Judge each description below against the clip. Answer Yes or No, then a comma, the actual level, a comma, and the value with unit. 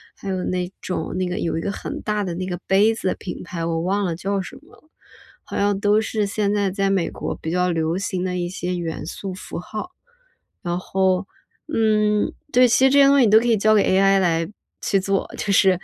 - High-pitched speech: Yes, high, 195 Hz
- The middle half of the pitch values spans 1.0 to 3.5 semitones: Yes, average, 2.7 semitones